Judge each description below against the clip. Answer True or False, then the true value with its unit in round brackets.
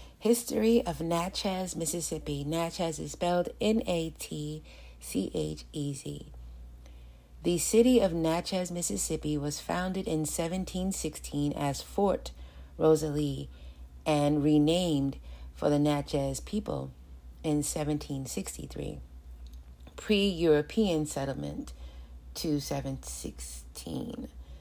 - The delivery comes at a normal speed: False (95 wpm)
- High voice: False (145 Hz)